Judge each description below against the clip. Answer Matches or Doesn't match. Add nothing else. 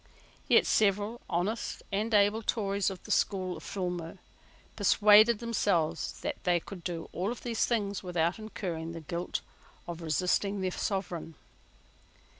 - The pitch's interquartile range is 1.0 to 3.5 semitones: Matches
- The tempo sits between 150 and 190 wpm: Doesn't match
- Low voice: Doesn't match